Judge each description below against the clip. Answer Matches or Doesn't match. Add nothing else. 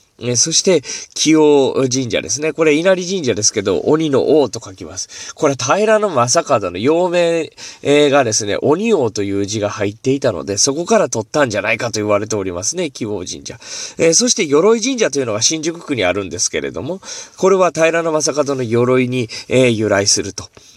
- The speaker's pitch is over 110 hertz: Matches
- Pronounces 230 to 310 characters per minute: Doesn't match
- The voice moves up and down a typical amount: Doesn't match